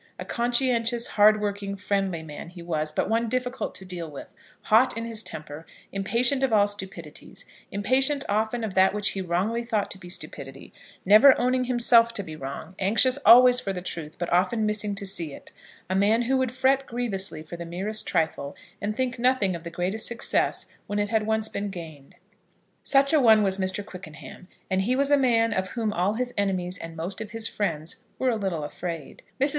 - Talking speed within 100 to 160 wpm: No, average, 200 wpm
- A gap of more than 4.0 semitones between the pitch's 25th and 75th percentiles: Yes, average, 4.8 semitones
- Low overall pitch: No, high, 205 Hz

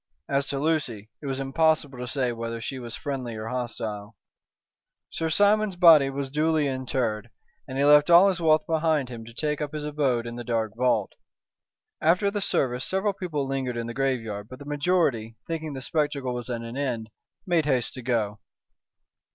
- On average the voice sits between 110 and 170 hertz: Yes, low, 135 Hz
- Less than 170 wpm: No, average, 185 wpm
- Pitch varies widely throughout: No, average, 4.6 semitones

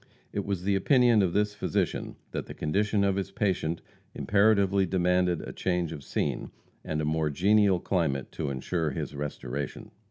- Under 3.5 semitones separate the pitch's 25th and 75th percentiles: No, average, 4.3 semitones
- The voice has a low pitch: Yes, very low, 90 Hz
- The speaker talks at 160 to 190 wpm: Yes, average, 165 wpm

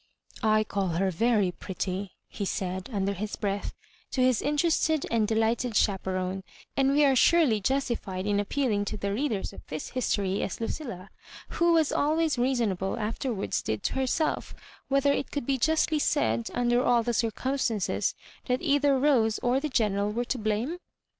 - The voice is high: Yes, high, 230 Hz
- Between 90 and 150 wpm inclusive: No, average, 165 wpm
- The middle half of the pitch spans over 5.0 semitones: Yes, wide, 5.4 semitones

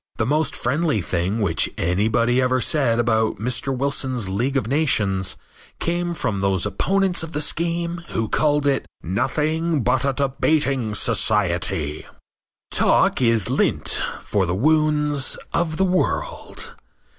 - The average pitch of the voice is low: Yes, low, 130 Hz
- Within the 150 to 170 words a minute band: No, slow, 135 wpm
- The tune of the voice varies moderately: No, wide, 6.2 semitones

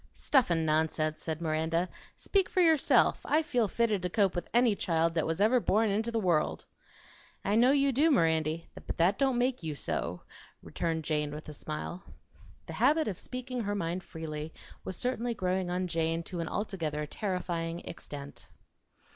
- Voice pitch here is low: No, medium, 180 Hz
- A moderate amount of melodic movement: No, wide, 6.4 semitones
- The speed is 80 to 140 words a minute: No, average, 175 wpm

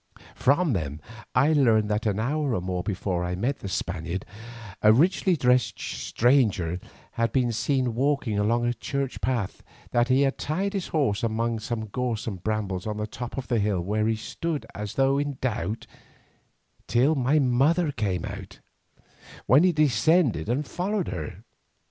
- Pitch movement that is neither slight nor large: Yes, average, 4.9 semitones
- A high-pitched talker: No, low, 120 Hz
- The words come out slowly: No, average, 170 wpm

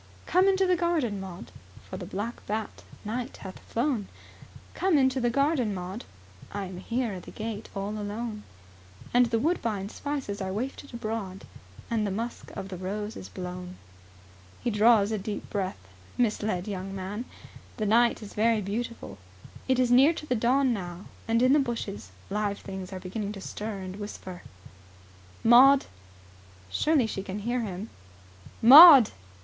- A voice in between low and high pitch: No, high, 215 Hz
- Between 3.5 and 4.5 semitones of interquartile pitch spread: Yes, average, 4.0 semitones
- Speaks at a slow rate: No, average, 160 wpm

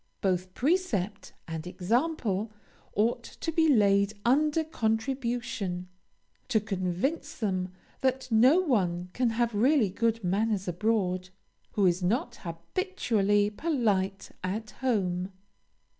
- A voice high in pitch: Yes, high, 215 Hz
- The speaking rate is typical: No, slow, 110 wpm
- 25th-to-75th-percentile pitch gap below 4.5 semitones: No, average, 5.1 semitones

